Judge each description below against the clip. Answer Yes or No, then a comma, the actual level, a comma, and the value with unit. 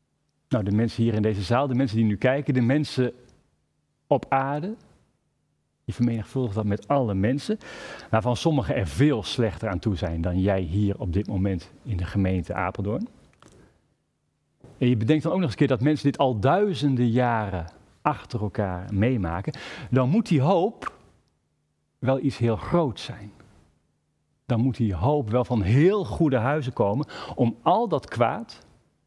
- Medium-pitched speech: No, low, 120 Hz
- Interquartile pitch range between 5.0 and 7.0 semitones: Yes, wide, 5.4 semitones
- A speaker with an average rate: Yes, average, 165 wpm